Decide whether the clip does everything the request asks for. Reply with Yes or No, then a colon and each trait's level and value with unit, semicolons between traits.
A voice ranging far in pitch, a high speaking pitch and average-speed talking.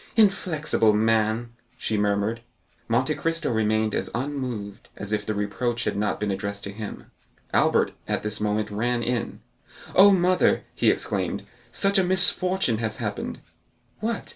No: wide, 6.4 semitones; low, 115 Hz; average, 145 wpm